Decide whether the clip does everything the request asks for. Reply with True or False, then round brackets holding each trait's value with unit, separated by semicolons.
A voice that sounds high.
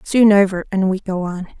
True (195 Hz)